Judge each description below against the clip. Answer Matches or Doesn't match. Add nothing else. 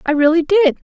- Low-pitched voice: Doesn't match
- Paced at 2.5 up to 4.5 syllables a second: Doesn't match